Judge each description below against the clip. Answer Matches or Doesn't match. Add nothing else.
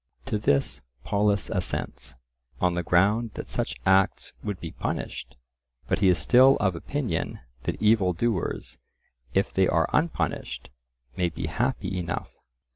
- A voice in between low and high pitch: Doesn't match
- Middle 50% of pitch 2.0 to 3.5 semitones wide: Doesn't match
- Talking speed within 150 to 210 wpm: Doesn't match